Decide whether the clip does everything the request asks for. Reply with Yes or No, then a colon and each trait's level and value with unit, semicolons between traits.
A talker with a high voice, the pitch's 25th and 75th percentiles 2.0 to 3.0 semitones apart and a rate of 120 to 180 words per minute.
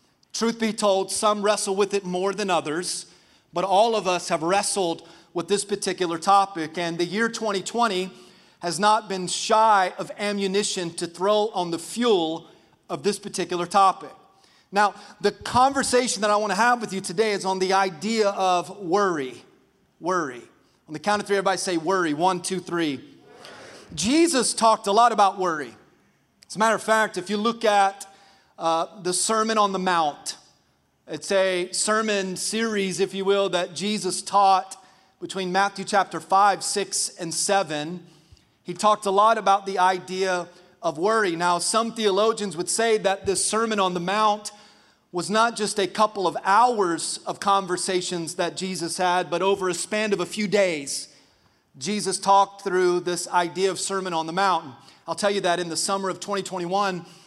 Yes: high, 195 Hz; narrow, 2.6 semitones; average, 175 wpm